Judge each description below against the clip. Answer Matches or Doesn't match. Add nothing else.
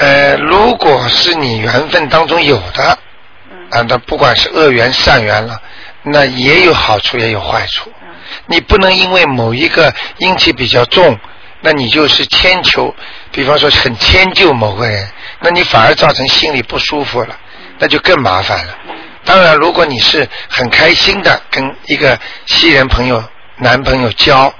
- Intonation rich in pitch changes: Matches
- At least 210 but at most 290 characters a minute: Matches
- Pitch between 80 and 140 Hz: Matches